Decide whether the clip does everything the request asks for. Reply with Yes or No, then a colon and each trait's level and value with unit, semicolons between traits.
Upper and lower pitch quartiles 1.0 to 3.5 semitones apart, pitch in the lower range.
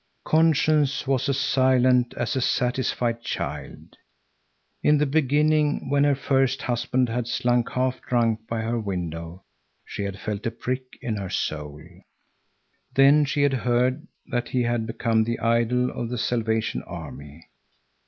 Yes: average, 2.9 semitones; low, 125 Hz